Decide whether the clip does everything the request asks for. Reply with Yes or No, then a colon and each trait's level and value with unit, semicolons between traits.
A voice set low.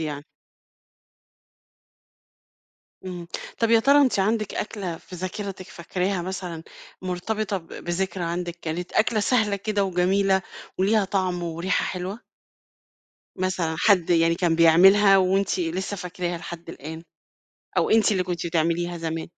No: medium, 185 Hz